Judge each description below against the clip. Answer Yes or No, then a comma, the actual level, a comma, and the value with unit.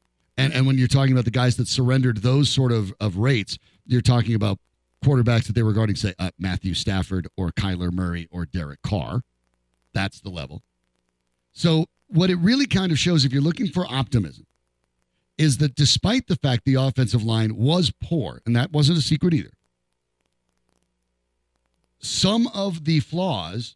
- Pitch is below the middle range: Yes, low, 115 Hz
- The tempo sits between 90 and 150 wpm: No, average, 170 wpm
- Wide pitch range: Yes, wide, 8.7 semitones